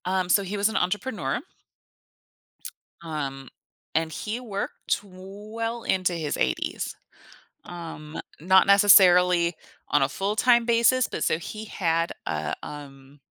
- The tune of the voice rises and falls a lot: No, average, 4.7 semitones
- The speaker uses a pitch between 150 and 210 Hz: Yes, medium, 185 Hz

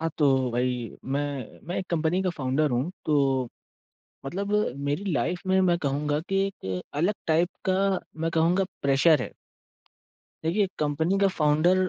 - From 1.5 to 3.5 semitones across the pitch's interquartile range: No, average, 4.5 semitones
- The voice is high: No, medium, 155 Hz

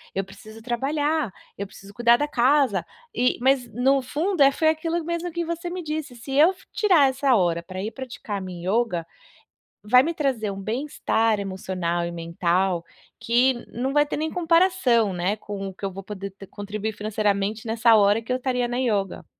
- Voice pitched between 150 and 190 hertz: No, high, 235 Hz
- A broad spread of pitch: Yes, wide, 6.5 semitones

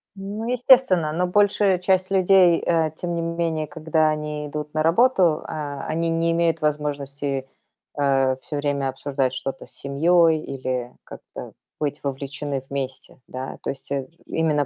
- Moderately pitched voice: Yes, medium, 155 Hz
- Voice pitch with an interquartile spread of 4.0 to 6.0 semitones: No, average, 3.5 semitones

